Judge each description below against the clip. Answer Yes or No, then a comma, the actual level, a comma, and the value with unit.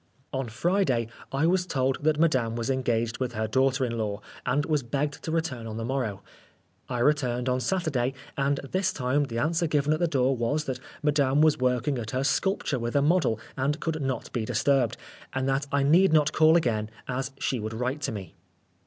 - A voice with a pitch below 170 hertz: Yes, low, 135 Hz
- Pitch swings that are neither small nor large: Yes, average, 3.7 semitones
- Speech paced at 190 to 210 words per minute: Yes, fast, 205 wpm